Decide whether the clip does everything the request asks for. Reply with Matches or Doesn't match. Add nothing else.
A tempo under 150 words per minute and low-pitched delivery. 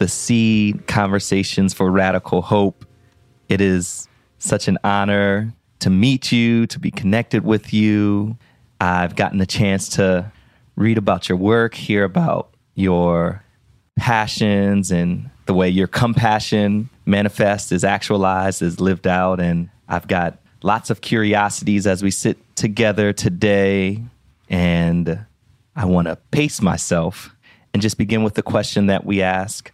Matches